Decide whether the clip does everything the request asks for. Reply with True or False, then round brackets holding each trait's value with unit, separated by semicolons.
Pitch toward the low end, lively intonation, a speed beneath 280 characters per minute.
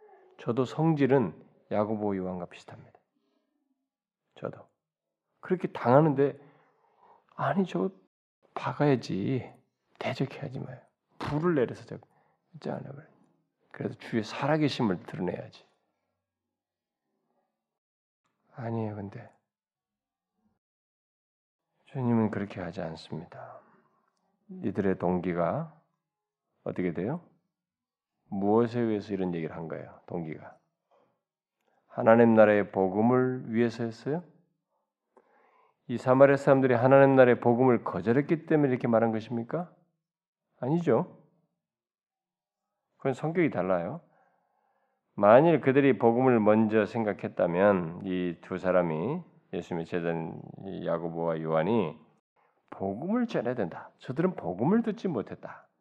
True (125 Hz; 8.1 semitones; 240 characters per minute)